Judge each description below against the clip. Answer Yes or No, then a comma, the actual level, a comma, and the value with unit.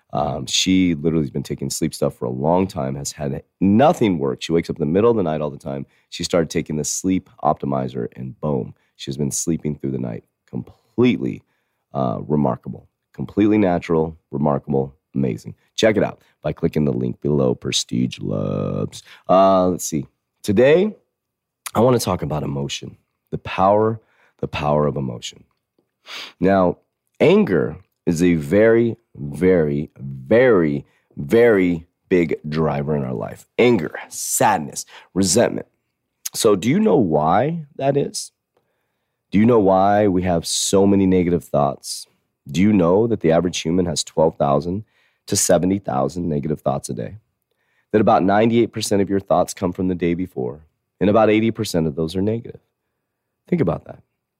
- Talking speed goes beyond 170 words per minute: No, average, 160 wpm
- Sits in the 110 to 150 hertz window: No, very low, 85 Hz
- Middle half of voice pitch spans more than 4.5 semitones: Yes, average, 5.1 semitones